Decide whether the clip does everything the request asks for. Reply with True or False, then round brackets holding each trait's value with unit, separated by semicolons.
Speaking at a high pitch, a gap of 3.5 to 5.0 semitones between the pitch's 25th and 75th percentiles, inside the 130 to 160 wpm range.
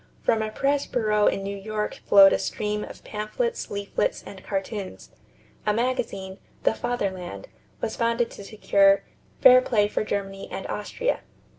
False (210 Hz; 2.9 semitones; 150 wpm)